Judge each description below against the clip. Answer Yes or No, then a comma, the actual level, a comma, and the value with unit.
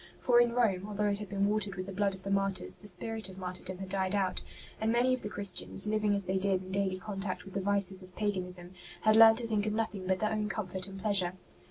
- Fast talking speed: Yes, fast, 260 wpm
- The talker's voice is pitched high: Yes, high, 200 Hz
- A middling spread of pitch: No, narrow, 2.2 semitones